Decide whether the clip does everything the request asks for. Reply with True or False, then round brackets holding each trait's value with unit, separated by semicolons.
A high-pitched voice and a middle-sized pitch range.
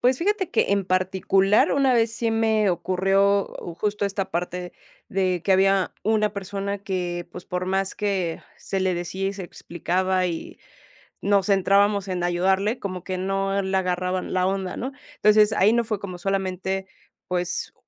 False (195 Hz; 1.8 semitones)